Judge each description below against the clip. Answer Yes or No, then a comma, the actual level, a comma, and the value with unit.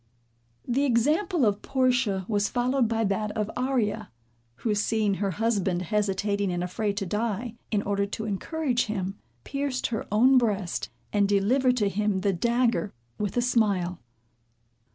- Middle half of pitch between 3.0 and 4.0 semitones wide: Yes, average, 3.5 semitones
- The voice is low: No, high, 215 Hz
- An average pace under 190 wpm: Yes, average, 150 wpm